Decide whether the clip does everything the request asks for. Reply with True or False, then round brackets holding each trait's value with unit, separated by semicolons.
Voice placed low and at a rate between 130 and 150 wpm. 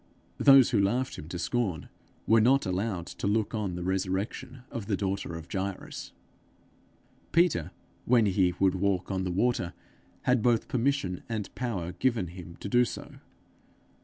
False (100 Hz; 160 wpm)